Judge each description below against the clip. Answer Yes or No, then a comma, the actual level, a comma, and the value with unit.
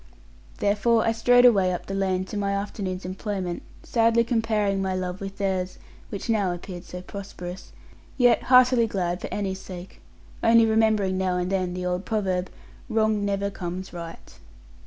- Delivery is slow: No, average, 160 wpm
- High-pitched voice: Yes, high, 195 Hz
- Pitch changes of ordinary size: Yes, average, 3.1 semitones